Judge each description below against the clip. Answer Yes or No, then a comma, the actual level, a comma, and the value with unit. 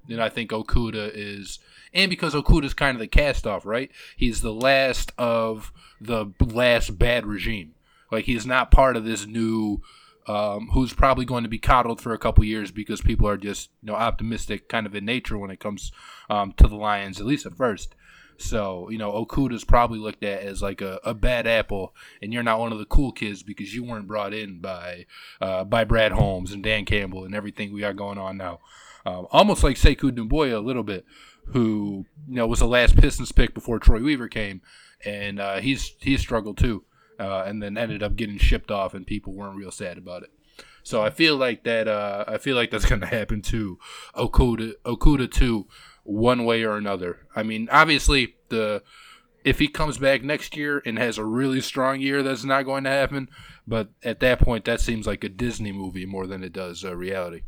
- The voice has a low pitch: Yes, low, 110 Hz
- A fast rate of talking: Yes, fast, 210 wpm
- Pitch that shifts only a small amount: No, average, 3.2 semitones